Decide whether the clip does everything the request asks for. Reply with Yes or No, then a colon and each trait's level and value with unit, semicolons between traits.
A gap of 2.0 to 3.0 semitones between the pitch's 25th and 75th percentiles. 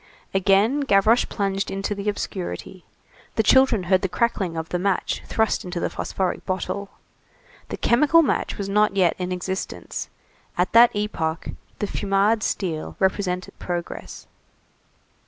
Yes: narrow, 2.5 semitones